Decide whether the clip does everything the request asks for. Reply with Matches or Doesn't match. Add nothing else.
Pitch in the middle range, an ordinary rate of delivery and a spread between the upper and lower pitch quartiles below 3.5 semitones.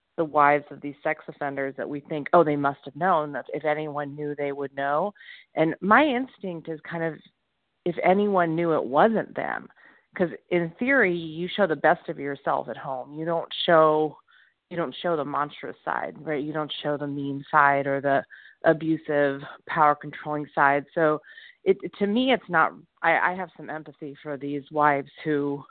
Matches